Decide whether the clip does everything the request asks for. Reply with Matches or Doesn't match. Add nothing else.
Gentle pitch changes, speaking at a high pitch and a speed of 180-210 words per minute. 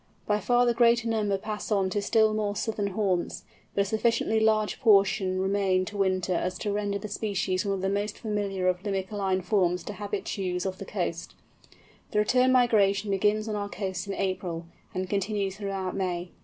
Matches